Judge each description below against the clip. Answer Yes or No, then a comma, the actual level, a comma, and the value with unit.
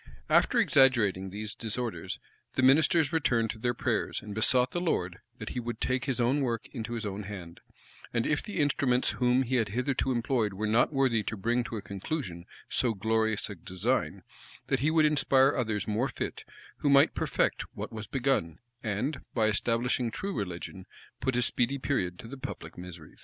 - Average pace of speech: Yes, average, 185 wpm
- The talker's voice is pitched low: Yes, low, 120 Hz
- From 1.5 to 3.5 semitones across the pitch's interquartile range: No, average, 4.0 semitones